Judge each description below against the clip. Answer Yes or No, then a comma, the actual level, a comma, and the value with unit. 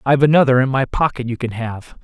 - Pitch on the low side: Yes, low, 130 Hz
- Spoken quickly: Yes, fast, 235 wpm